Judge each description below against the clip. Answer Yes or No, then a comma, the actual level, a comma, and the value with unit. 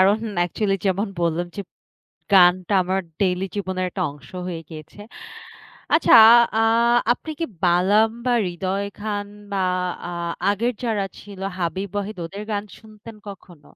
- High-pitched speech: Yes, high, 195 Hz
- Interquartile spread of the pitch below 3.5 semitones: Yes, narrow, 2.6 semitones